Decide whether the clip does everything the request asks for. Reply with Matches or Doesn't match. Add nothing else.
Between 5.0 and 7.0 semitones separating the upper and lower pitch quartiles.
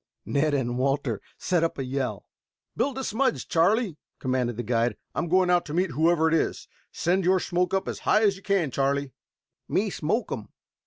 Matches